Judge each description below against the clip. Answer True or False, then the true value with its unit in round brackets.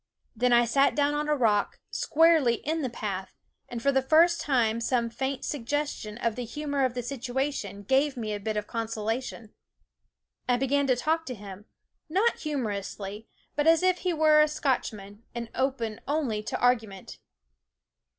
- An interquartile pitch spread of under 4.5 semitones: False (4.9 semitones)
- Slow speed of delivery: False (170 wpm)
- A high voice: True (250 Hz)